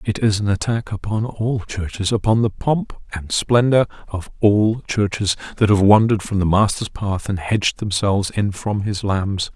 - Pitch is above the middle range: No, low, 105 Hz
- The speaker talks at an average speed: Yes, average, 180 wpm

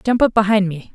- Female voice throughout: Yes, female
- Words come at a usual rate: No, fast, 255 wpm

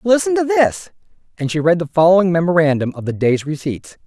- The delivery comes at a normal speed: Yes, average, 190 wpm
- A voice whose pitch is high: No, medium, 175 Hz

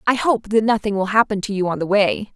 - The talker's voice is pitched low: No, high, 205 Hz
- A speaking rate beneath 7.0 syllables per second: Yes, 5.9 syllables/s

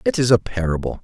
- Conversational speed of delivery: No, fast, 230 wpm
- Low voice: Yes, low, 100 Hz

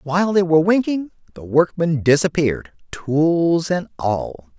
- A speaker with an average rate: No, slow, 130 wpm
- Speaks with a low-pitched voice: No, medium, 160 Hz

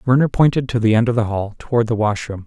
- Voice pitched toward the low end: Yes, low, 115 Hz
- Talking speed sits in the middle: No, fast, 270 wpm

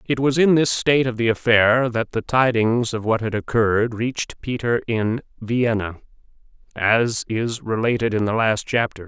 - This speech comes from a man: Yes, male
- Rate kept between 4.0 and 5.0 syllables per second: Yes, 4.7 syllables/s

